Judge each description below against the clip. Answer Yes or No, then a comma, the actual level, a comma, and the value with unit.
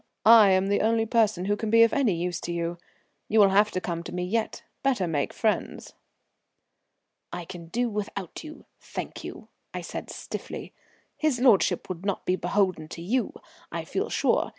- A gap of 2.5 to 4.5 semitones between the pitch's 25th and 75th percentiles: Yes, average, 4.1 semitones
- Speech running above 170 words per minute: Yes, average, 185 wpm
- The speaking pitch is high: Yes, high, 200 Hz